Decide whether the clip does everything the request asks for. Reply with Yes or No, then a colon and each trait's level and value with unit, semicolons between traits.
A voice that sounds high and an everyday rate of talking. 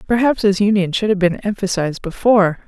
Yes: high, 200 Hz; average, 180 wpm